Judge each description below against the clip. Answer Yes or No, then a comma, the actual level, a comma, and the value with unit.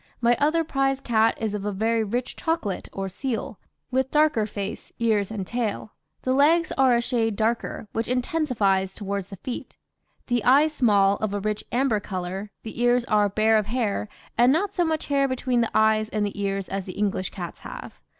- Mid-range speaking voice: No, high, 225 Hz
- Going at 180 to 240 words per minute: Yes, average, 195 wpm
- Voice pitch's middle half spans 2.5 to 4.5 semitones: Yes, average, 4.1 semitones